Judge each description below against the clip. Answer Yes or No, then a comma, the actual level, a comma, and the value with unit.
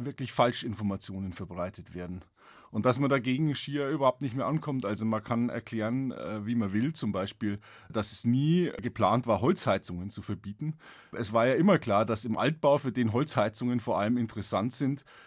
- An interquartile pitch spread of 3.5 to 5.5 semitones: Yes, average, 4.7 semitones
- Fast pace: No, average, 175 wpm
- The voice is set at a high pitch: No, low, 120 Hz